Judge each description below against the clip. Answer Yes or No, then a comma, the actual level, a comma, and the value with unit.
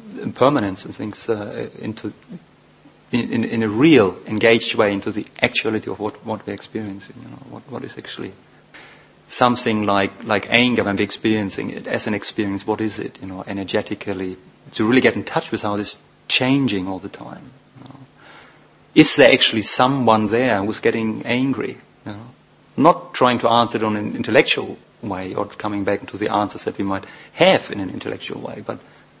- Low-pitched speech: Yes, low, 110 Hz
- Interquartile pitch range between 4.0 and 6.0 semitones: No, narrow, 2.4 semitones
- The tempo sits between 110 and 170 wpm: No, average, 190 wpm